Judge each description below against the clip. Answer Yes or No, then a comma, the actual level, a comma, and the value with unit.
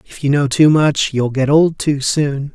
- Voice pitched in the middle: Yes, medium, 145 Hz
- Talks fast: Yes, fast, 235 wpm